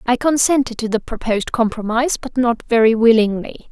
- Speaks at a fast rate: No, average, 145 wpm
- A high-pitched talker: Yes, high, 235 Hz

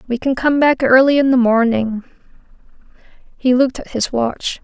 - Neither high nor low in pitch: No, very high, 250 Hz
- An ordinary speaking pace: Yes, average, 170 wpm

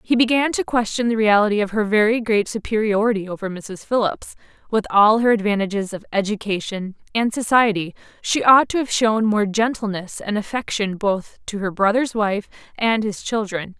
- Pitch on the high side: Yes, high, 215 Hz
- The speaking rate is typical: Yes, average, 170 wpm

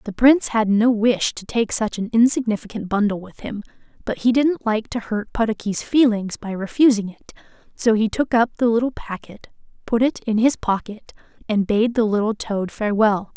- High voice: Yes, high, 220 Hz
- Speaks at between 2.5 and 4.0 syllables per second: No, 5.2 syllables/s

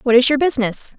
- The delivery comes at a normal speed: No, fast, 245 wpm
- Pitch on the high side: Yes, very high, 255 Hz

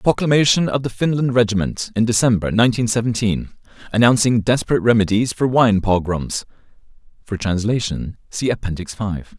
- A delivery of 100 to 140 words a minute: Yes, slow, 135 wpm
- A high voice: No, low, 110 Hz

